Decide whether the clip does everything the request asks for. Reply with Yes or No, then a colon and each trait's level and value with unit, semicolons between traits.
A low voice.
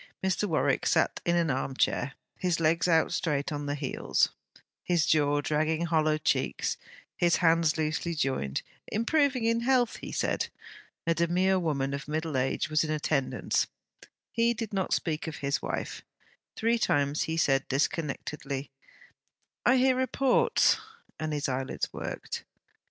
No: medium, 160 Hz